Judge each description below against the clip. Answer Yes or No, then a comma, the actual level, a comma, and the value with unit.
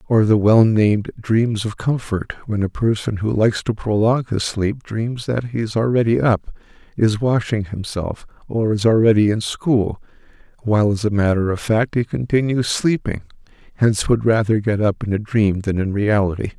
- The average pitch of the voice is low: Yes, low, 110 Hz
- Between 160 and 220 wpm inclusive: Yes, average, 180 wpm